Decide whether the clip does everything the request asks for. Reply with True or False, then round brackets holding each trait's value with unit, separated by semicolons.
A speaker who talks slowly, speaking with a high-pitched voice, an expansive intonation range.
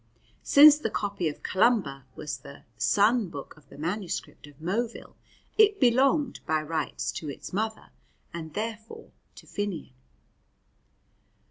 True (130 wpm; 200 Hz; 7.1 semitones)